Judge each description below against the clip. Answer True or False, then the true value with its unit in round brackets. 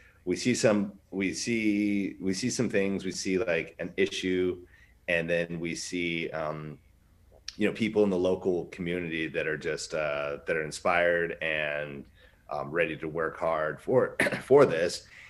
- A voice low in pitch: True (90 Hz)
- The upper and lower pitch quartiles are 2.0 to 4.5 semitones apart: True (2.8 semitones)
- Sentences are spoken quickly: False (165 wpm)